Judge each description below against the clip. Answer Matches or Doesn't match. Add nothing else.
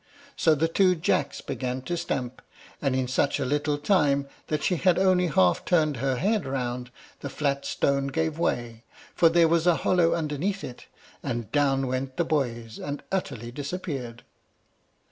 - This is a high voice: Doesn't match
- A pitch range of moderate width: Matches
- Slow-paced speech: Doesn't match